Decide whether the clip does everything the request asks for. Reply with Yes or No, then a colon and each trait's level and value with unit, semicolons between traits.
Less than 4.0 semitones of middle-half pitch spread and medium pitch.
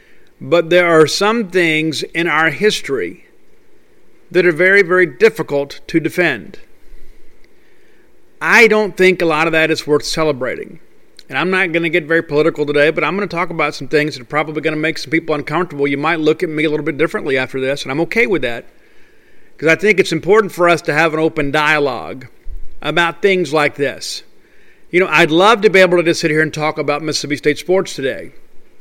No: average, 4.5 semitones; medium, 165 Hz